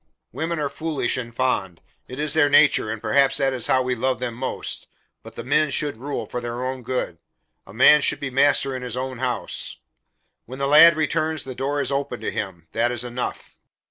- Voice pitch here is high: No, low, 130 Hz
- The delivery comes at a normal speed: No, fast, 210 wpm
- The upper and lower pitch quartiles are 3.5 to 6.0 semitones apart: No, average, 2.8 semitones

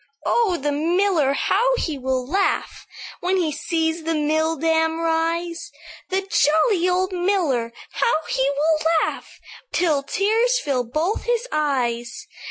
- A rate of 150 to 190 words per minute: No, average, 140 wpm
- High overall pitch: Yes, very high, 325 Hz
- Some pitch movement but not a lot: Yes, average, 4.2 semitones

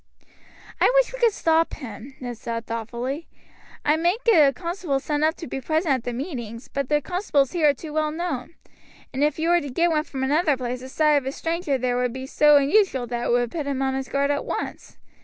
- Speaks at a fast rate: Yes, fast, 235 wpm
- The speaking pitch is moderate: No, very high, 285 Hz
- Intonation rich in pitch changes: No, average, 4.0 semitones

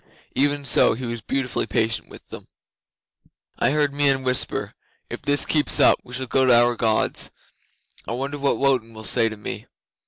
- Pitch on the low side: Yes, low, 130 Hz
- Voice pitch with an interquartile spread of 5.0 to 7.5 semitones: No, average, 3.1 semitones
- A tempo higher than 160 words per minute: Yes, average, 180 wpm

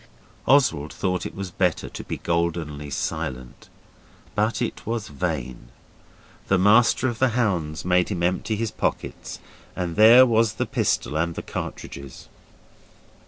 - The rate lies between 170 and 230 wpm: No, average, 140 wpm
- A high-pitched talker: No, very low, 90 Hz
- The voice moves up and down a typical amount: No, wide, 5.9 semitones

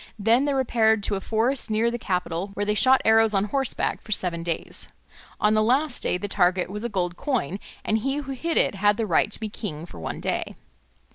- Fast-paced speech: Yes, fast, 225 wpm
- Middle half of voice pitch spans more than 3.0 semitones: Yes, average, 3.9 semitones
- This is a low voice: No, high, 215 Hz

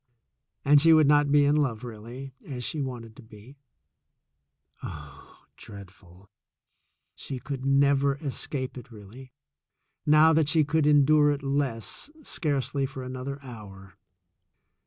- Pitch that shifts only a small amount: No, average, 4.1 semitones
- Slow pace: Yes, slow, 130 wpm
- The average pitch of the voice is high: No, low, 135 Hz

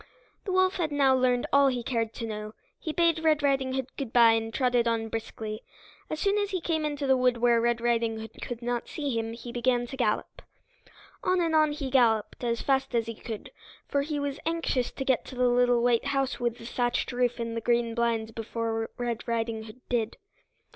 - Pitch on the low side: No, high, 245 Hz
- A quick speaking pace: Yes, fast, 215 wpm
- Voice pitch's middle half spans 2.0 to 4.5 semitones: Yes, average, 3.2 semitones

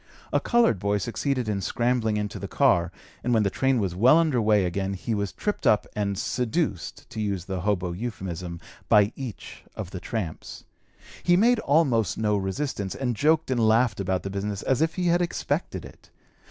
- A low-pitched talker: Yes, low, 110 Hz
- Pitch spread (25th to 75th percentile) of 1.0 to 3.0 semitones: No, average, 5.1 semitones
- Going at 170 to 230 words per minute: Yes, average, 190 wpm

